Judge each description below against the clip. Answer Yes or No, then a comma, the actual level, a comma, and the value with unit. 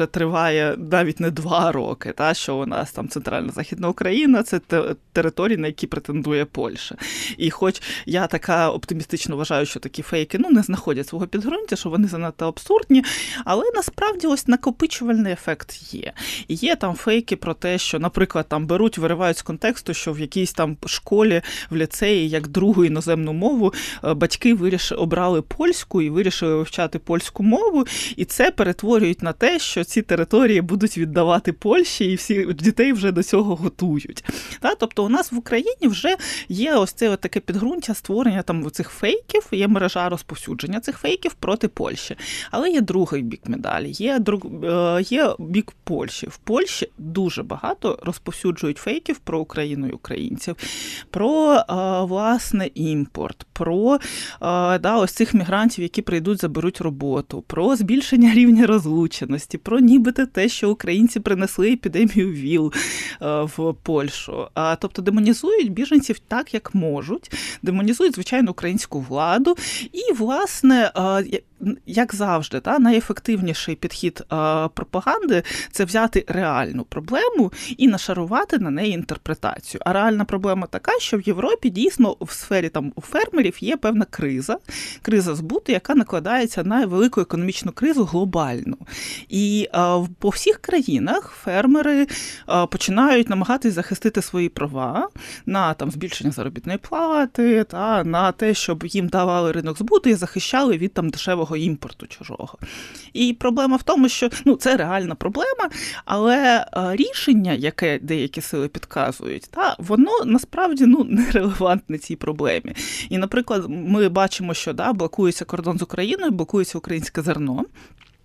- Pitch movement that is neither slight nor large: No, wide, 5.9 semitones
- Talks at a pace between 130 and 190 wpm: Yes, average, 145 wpm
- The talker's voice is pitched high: Yes, high, 195 Hz